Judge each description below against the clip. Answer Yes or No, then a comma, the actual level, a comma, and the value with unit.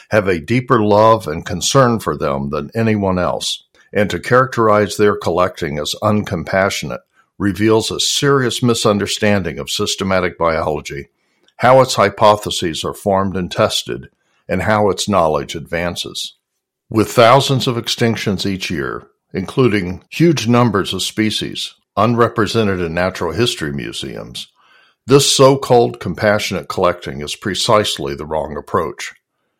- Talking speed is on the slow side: Yes, slow, 130 wpm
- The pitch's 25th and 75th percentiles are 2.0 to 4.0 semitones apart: No, average, 4.7 semitones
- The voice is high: No, low, 105 Hz